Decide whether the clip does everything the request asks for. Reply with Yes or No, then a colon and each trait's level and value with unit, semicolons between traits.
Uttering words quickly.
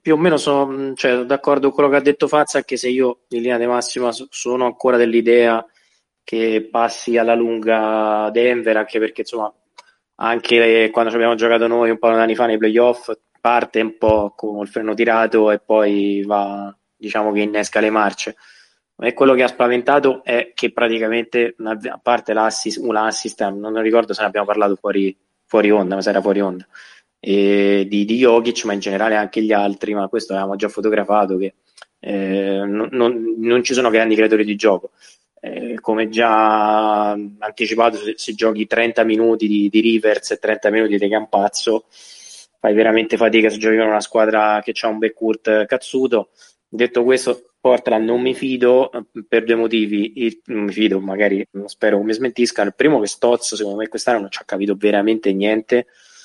Yes: fast, 185 wpm